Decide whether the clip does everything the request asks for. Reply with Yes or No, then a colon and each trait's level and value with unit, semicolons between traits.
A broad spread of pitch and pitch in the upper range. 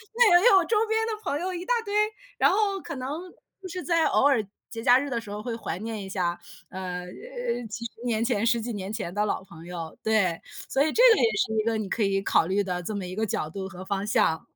Yes: wide, 7.1 semitones; high, 220 Hz